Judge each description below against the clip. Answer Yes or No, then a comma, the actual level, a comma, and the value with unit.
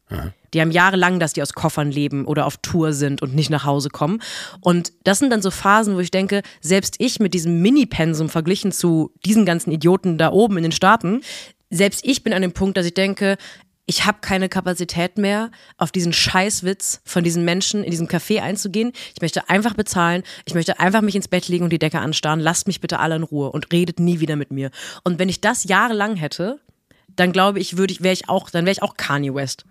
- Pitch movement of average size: Yes, average, 3.2 semitones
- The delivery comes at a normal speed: No, fast, 230 wpm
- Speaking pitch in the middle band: Yes, medium, 180 Hz